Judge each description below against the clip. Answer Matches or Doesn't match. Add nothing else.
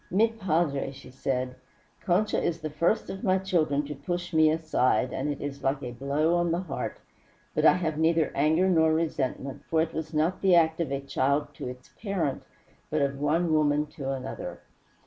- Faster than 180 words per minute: Matches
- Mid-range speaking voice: Matches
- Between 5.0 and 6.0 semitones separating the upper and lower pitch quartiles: Doesn't match